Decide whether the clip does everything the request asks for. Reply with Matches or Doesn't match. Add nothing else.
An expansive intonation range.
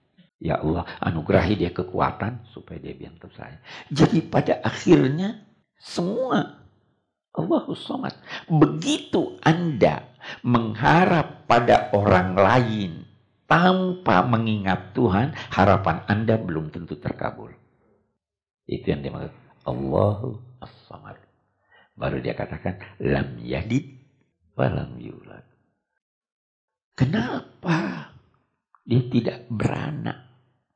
Matches